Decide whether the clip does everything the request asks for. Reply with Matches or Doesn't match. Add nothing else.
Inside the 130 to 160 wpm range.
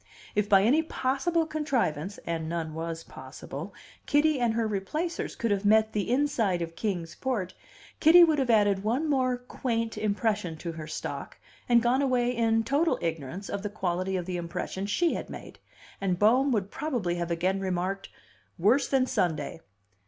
Doesn't match